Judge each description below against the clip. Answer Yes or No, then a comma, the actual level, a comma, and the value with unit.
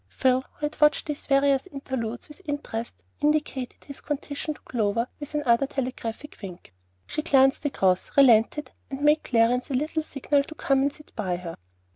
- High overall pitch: Yes, very high, 275 Hz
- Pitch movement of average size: Yes, average, 4.1 semitones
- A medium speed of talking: Yes, average, 170 wpm